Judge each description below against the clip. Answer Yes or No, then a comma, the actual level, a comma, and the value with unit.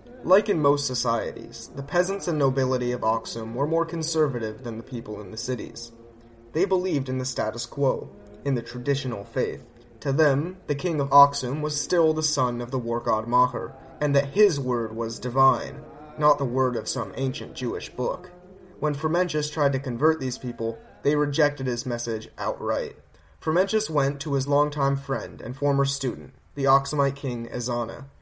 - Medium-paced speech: Yes, average, 175 wpm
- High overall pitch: No, low, 135 Hz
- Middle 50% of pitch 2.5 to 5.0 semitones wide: Yes, average, 3.7 semitones